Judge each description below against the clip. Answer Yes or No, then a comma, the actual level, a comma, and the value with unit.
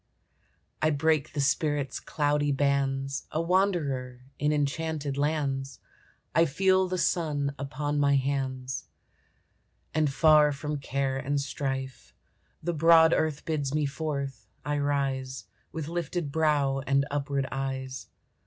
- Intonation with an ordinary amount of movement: No, narrow, 2.2 semitones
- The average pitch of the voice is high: No, medium, 145 Hz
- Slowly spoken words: Yes, slow, 125 wpm